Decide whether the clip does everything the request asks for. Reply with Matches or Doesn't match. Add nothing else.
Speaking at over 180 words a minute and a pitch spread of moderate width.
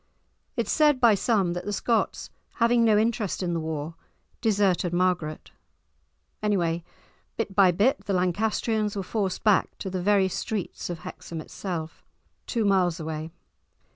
Doesn't match